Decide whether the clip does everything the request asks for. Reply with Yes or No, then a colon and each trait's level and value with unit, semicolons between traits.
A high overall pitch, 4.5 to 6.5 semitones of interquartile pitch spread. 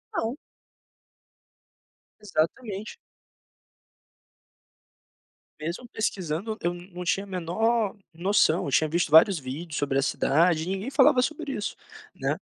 No: medium, 180 Hz; average, 5.2 semitones